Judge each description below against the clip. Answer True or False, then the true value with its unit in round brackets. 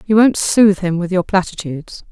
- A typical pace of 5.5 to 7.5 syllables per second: True (5.6 syllables/s)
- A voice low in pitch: False (190 Hz)